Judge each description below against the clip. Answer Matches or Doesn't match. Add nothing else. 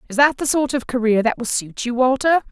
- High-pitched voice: Matches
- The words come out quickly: Matches